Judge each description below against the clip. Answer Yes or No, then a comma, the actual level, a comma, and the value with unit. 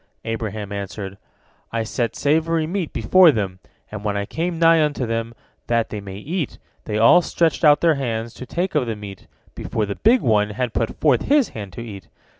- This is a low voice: Yes, low, 115 Hz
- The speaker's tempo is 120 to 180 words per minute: No, average, 200 wpm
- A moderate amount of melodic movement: No, wide, 7.2 semitones